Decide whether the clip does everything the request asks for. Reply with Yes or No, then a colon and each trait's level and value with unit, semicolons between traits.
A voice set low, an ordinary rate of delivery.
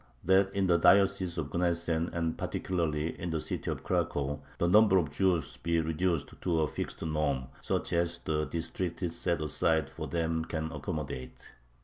Yes: very low, 85 Hz; average, 165 wpm